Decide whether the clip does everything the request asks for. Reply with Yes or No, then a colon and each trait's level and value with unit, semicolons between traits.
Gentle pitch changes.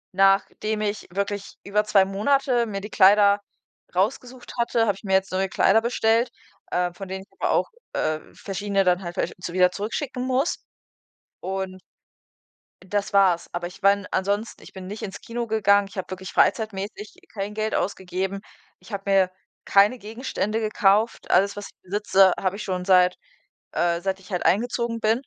Yes: narrow, 2.3 semitones